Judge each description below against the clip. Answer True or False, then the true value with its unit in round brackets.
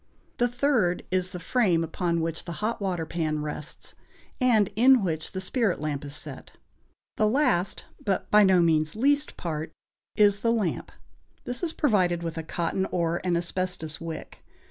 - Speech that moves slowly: False (165 wpm)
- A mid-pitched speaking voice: True (180 Hz)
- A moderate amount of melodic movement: True (4.6 semitones)